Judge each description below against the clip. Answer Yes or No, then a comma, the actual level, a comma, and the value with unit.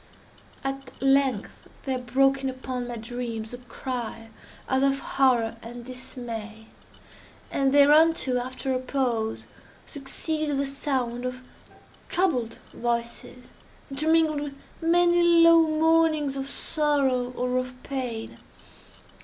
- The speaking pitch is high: Yes, very high, 265 Hz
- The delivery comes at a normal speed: No, slow, 110 wpm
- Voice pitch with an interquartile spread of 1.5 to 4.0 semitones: Yes, average, 2.9 semitones